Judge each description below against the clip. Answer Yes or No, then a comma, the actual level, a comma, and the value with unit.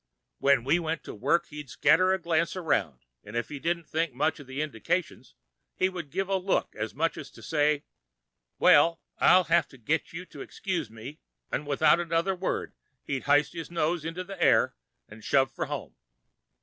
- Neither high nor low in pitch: Yes, medium, 160 Hz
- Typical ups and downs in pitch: Yes, average, 3.7 semitones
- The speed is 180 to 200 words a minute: Yes, average, 190 wpm